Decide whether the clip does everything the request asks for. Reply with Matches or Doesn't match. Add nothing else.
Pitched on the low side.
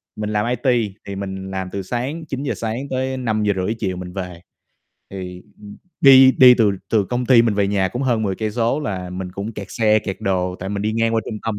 Matches